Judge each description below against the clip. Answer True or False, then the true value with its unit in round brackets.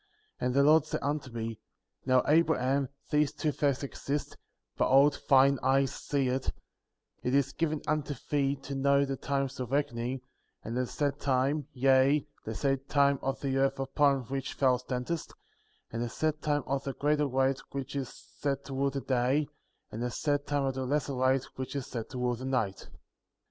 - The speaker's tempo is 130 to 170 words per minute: False (190 wpm)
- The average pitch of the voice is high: False (135 Hz)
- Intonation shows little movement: True (1.7 semitones)